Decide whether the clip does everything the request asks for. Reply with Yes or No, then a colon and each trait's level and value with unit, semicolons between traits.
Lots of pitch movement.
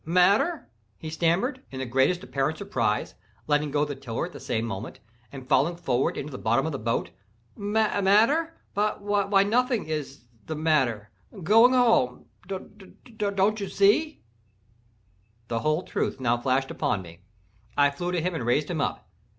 Yes: wide, 7.7 semitones